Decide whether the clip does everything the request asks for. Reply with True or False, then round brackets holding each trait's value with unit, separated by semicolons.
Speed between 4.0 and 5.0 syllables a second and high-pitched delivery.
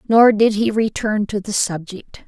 True (4.3 syllables/s; 210 Hz)